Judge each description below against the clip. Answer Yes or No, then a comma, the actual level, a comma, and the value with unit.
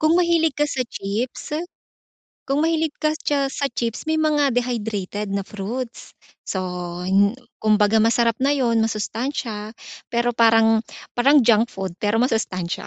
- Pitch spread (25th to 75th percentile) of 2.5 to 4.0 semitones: No, average, 4.7 semitones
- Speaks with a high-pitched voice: Yes, high, 235 Hz